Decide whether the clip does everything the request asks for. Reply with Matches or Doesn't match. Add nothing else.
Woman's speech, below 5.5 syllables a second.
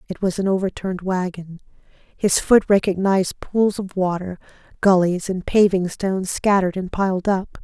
Matches